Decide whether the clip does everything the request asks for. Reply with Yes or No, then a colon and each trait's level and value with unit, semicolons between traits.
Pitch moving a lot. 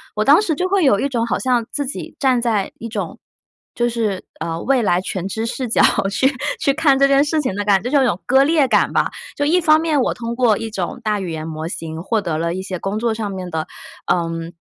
Yes: wide, 6.4 semitones